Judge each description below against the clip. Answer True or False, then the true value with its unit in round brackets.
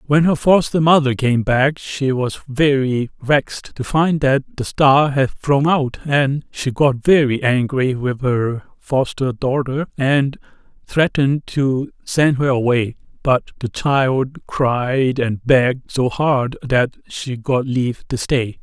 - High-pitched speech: False (135 Hz)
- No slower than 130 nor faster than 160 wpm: True (150 wpm)